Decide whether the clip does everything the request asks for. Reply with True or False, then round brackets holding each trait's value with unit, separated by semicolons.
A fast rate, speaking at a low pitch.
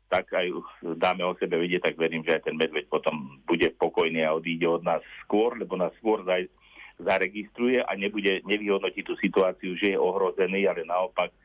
True (180 wpm; 95 Hz)